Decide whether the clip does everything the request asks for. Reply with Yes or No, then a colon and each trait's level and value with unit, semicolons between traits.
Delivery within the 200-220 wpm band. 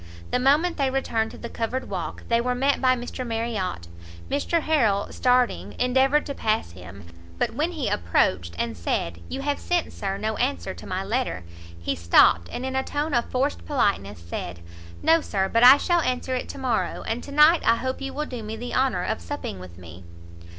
Yes: fast, 205 wpm